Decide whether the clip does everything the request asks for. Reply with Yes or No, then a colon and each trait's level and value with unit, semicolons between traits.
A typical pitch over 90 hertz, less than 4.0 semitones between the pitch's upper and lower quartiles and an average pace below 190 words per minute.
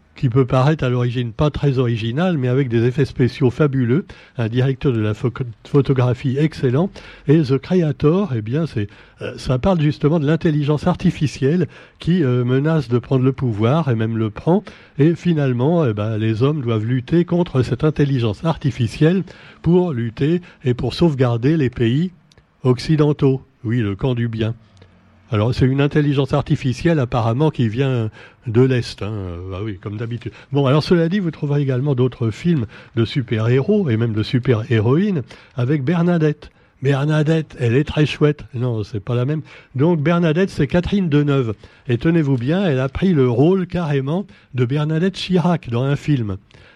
No: low, 135 Hz; average, 4.5 semitones; average, 170 wpm